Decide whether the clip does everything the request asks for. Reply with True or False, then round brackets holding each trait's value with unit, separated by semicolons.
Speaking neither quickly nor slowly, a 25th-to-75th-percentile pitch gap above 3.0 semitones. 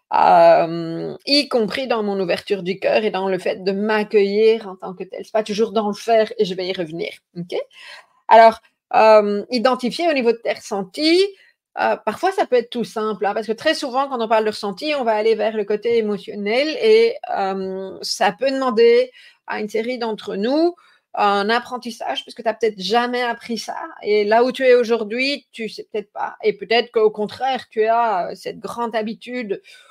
True (205 wpm; 4.1 semitones)